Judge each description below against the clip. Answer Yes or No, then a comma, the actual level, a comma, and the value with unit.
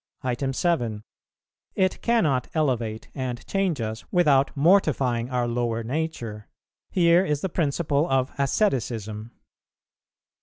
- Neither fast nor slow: No, slow, 105 wpm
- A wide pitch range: Yes, wide, 5.8 semitones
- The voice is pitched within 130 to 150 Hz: Yes, low, 135 Hz